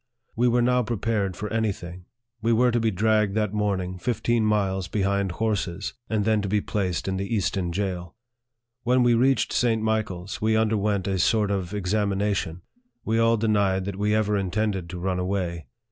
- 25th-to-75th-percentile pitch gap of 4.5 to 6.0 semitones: No, average, 2.7 semitones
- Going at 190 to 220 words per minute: No, average, 180 wpm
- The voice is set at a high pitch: No, low, 105 Hz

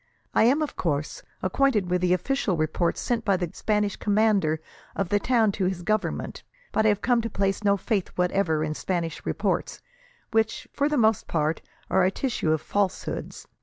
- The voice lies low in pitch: No, high, 195 Hz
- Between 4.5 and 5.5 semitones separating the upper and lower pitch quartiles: No, average, 3.9 semitones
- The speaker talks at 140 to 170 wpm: No, average, 185 wpm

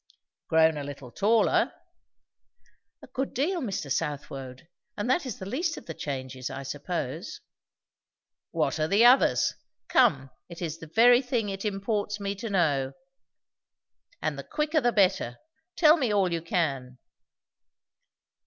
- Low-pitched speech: No, high, 195 Hz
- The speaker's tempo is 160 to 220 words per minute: No, average, 145 wpm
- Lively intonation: Yes, wide, 8.7 semitones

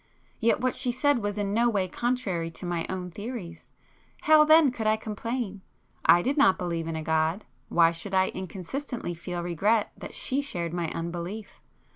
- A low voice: No, high, 195 Hz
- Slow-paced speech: No, average, 175 wpm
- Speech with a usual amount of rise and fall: No, wide, 5.8 semitones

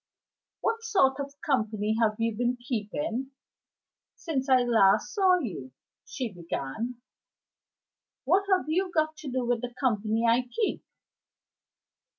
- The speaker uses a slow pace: Yes, slow, 130 wpm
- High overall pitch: Yes, very high, 250 Hz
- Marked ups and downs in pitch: Yes, wide, 5.7 semitones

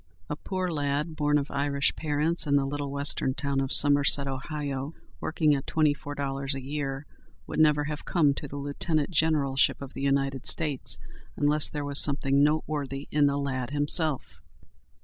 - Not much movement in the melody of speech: Yes, narrow, 1.4 semitones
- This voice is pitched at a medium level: Yes, medium, 145 Hz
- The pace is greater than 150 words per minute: Yes, average, 170 wpm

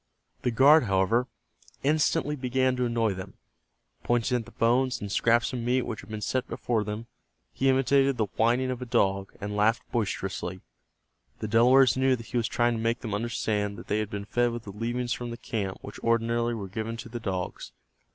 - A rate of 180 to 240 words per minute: Yes, average, 200 wpm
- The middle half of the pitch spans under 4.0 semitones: Yes, average, 2.9 semitones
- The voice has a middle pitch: No, low, 115 Hz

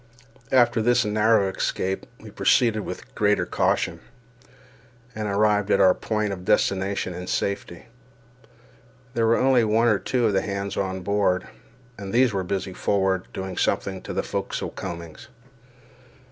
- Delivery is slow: No, average, 145 wpm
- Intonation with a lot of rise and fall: No, narrow, 2.6 semitones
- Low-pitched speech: Yes, low, 100 Hz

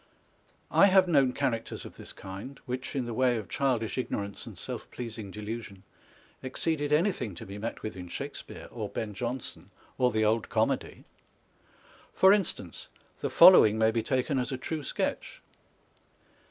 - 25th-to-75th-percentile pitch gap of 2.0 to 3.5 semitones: No, average, 4.1 semitones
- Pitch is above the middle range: No, low, 120 Hz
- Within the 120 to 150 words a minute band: No, average, 160 wpm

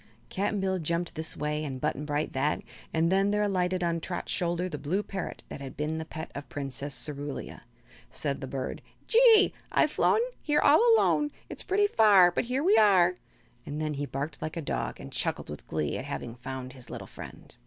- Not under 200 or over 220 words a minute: Yes, fast, 205 wpm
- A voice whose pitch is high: No, medium, 160 Hz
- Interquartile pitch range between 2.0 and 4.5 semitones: No, average, 5.1 semitones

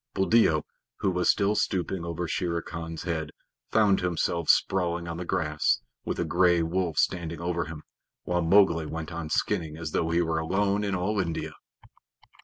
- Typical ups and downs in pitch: No, narrow, 2.2 semitones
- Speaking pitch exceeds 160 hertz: No, very low, 85 Hz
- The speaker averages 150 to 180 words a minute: Yes, average, 170 wpm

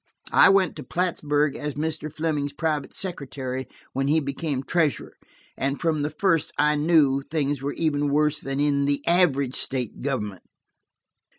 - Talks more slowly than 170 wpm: Yes, average, 150 wpm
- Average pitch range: No, narrow, 2.3 semitones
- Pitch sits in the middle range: Yes, medium, 145 Hz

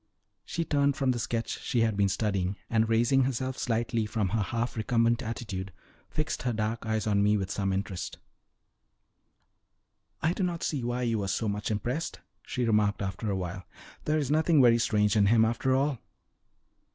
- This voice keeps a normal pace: Yes, average, 180 wpm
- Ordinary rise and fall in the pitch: Yes, average, 3.4 semitones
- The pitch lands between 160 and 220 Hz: No, low, 115 Hz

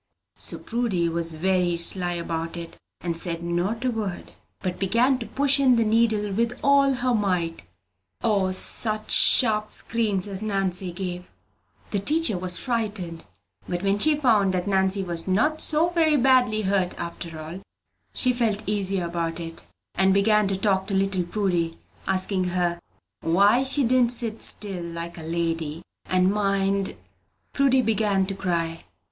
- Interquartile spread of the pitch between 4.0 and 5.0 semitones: Yes, average, 4.4 semitones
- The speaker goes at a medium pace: Yes, average, 155 wpm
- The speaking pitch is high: Yes, high, 195 Hz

